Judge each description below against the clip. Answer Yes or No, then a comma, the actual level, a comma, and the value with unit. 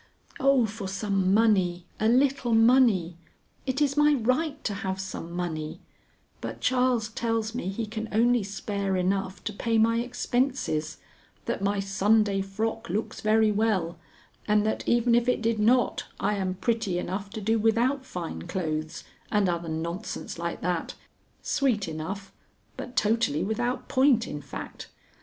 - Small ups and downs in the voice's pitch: No, average, 3.8 semitones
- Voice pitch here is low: No, high, 215 Hz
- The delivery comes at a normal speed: Yes, average, 150 wpm